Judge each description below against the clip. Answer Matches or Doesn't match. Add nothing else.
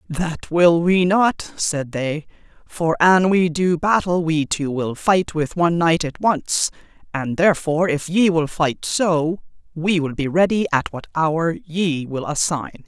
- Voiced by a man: Doesn't match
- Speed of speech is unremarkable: Matches